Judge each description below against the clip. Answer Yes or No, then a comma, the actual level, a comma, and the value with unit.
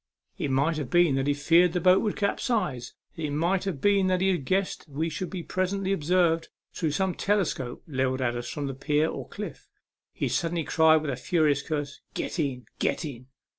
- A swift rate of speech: Yes, fast, 210 wpm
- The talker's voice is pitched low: No, medium, 160 Hz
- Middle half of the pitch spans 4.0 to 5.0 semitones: Yes, average, 4.5 semitones